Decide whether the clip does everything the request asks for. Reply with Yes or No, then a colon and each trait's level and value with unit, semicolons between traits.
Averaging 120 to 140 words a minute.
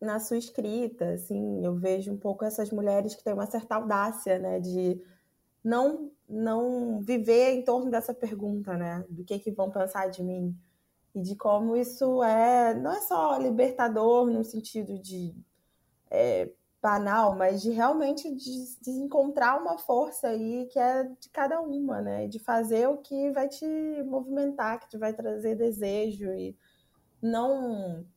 No: average, 160 wpm